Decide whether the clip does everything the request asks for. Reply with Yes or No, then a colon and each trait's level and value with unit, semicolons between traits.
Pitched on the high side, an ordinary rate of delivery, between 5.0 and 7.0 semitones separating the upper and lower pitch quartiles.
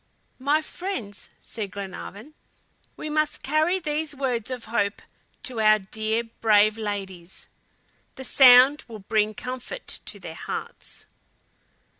No: high, 230 Hz; slow, 120 wpm; wide, 5.6 semitones